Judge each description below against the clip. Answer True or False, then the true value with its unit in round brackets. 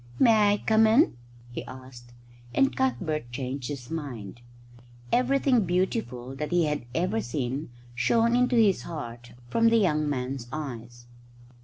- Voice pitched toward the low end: False (150 Hz)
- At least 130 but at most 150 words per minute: True (140 wpm)